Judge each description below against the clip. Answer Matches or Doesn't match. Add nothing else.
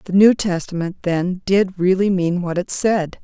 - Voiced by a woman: Matches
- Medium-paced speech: Matches